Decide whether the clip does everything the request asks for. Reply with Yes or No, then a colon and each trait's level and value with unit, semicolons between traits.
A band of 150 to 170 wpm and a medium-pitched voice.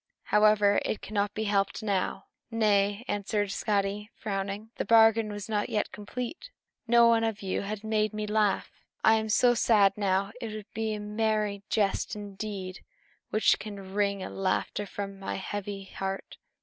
No: average, 160 wpm; high, 210 Hz